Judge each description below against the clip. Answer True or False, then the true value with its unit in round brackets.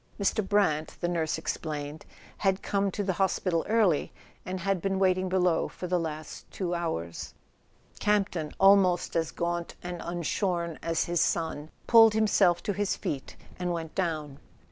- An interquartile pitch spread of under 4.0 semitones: True (3.0 semitones)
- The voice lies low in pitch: False (175 Hz)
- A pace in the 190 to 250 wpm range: False (165 wpm)